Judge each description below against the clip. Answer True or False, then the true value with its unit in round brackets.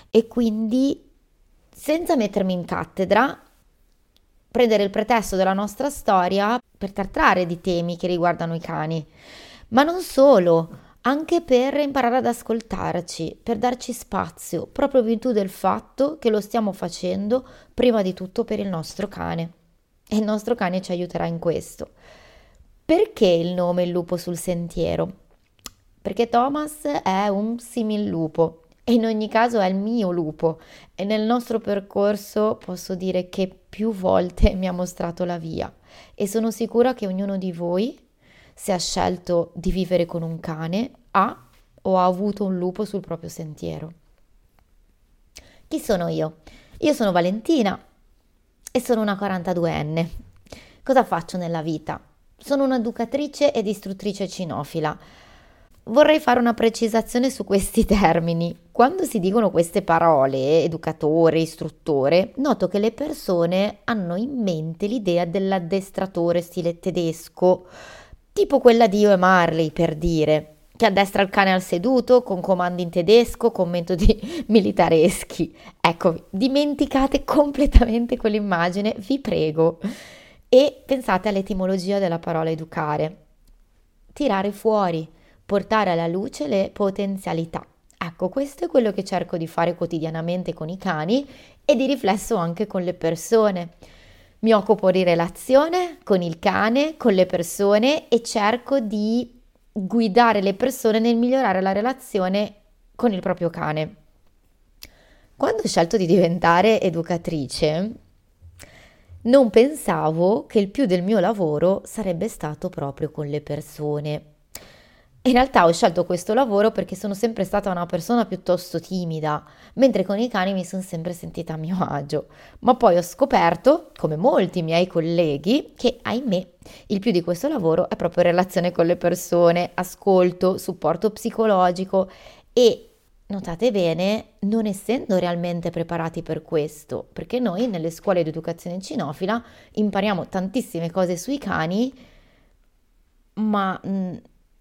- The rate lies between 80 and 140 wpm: True (135 wpm)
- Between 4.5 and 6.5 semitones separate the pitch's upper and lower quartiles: True (5.1 semitones)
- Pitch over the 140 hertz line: True (190 Hz)